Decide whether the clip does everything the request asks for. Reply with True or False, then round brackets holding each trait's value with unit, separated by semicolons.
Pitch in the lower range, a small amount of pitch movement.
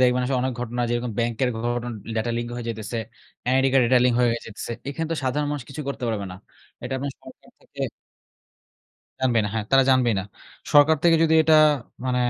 True (125 Hz; 2.2 semitones)